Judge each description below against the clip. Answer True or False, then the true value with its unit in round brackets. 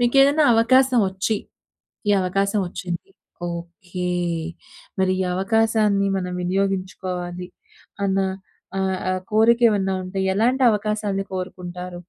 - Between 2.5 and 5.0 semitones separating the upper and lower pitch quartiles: True (3.2 semitones)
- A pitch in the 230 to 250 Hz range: False (195 Hz)